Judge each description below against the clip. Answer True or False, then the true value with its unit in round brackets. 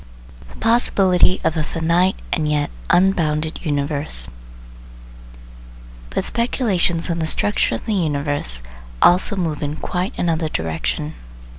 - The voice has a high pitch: False (160 Hz)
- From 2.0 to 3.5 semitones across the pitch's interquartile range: False (3.9 semitones)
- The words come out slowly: True (120 wpm)